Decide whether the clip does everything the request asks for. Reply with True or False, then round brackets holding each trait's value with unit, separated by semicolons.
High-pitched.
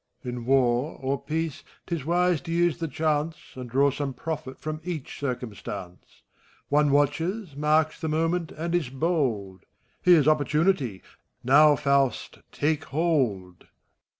False (150 Hz)